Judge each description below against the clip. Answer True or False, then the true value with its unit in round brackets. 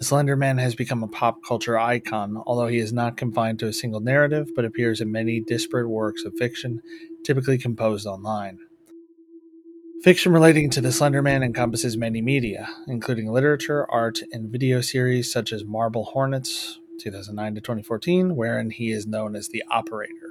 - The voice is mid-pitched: False (120 Hz)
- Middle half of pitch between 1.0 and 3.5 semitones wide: False (4.5 semitones)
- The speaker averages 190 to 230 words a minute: False (165 wpm)